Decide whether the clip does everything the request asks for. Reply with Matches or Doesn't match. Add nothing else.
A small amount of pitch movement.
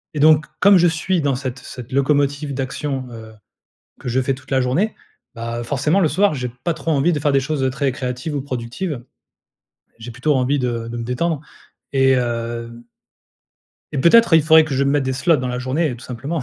Doesn't match